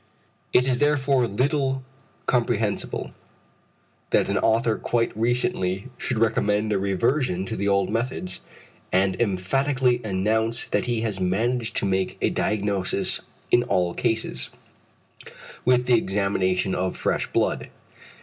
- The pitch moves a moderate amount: Yes, average, 4.2 semitones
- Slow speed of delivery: Yes, slow, 125 wpm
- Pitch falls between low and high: No, low, 110 Hz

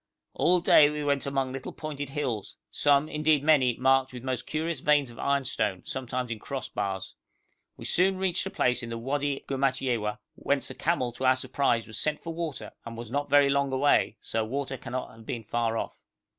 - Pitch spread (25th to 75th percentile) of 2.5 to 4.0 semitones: Yes, average, 3.2 semitones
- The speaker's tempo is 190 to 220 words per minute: Yes, average, 200 wpm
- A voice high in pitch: No, low, 135 Hz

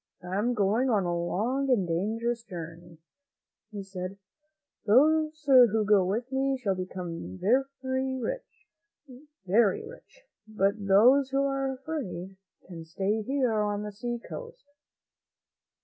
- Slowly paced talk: Yes, slow, 120 wpm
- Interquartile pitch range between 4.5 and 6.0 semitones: Yes, wide, 5.6 semitones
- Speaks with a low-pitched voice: No, high, 220 Hz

